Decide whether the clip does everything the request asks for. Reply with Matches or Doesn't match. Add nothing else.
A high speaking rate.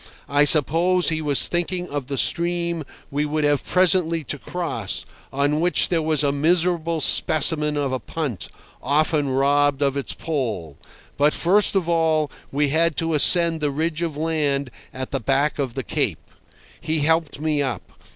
Doesn't match